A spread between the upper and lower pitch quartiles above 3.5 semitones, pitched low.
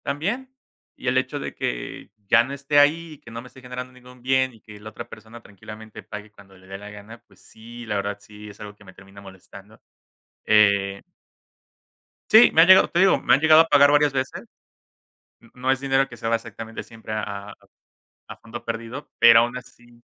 Yes: average, 4.2 semitones; low, 115 Hz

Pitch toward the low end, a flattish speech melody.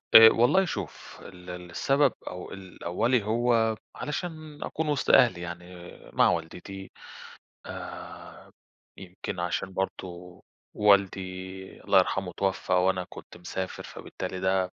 No: very low, 95 Hz; average, 3.9 semitones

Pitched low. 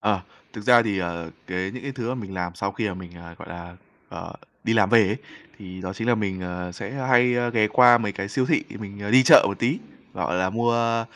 Yes: low, 105 Hz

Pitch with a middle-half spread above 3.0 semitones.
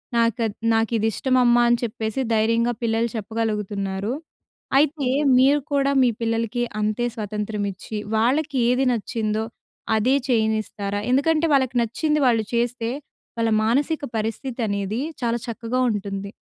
No: average, 2.7 semitones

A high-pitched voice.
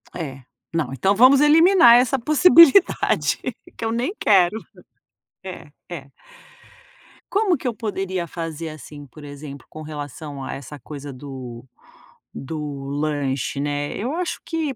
No: medium, 160 Hz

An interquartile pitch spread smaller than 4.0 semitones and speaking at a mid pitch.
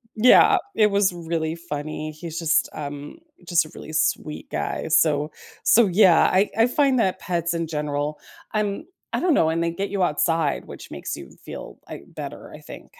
No: average, 4.4 semitones; medium, 170 Hz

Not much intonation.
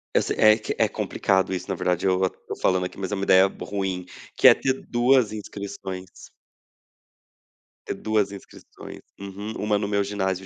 Yes: narrow, 1.8 semitones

